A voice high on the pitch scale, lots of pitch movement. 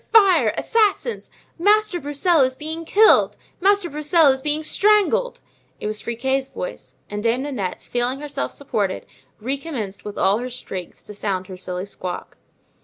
Yes: very high, 270 Hz; wide, 8.4 semitones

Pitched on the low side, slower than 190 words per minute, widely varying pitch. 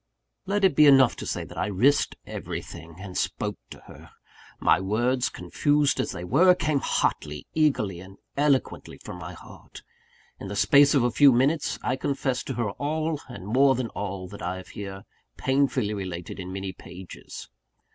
Yes: low, 120 Hz; average, 175 wpm; wide, 6.6 semitones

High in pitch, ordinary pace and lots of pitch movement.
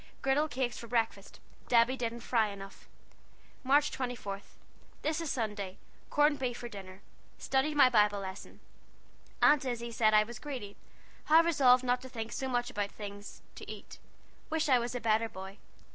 No: high, 240 Hz; average, 165 wpm; average, 4.1 semitones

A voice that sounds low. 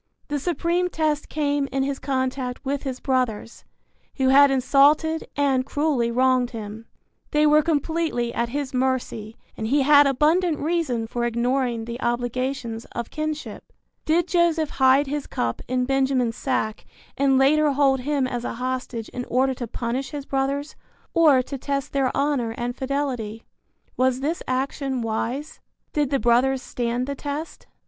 No: very high, 265 Hz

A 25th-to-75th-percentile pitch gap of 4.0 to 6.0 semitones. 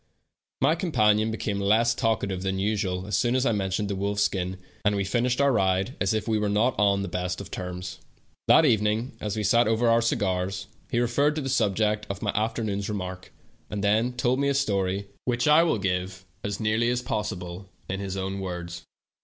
No: average, 3.5 semitones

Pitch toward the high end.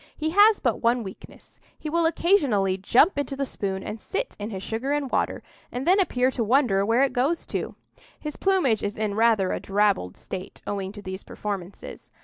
Yes: high, 230 Hz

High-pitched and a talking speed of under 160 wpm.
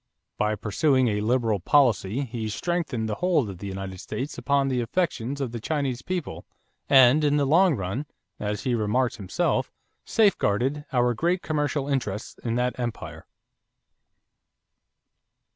No: low, 125 Hz; average, 145 wpm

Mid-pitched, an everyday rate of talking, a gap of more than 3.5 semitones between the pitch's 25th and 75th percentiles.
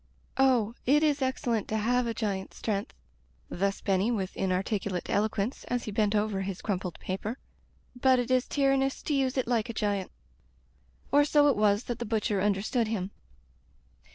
No: high, 220 Hz; average, 180 wpm; average, 4.2 semitones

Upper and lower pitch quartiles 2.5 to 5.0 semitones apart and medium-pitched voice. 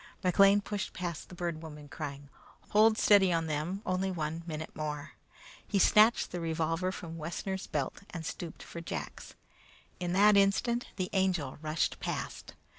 Yes: average, 3.7 semitones; medium, 175 Hz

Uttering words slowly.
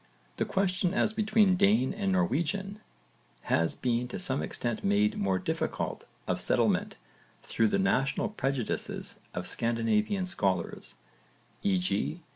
Yes: slow, 120 wpm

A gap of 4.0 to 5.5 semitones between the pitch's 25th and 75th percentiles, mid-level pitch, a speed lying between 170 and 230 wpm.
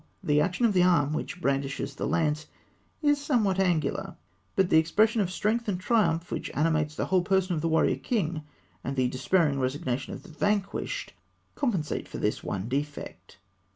Yes: average, 4.7 semitones; medium, 165 Hz; average, 175 wpm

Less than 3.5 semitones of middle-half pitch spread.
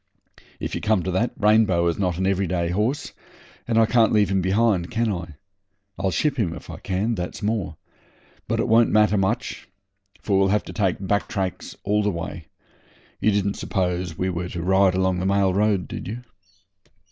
Yes: average, 2.9 semitones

